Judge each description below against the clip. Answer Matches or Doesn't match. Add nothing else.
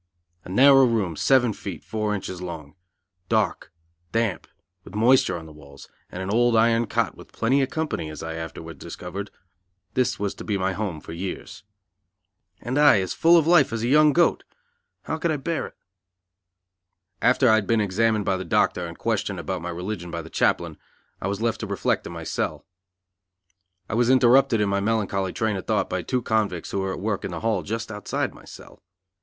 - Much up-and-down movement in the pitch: Doesn't match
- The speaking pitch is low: Matches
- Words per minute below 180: Doesn't match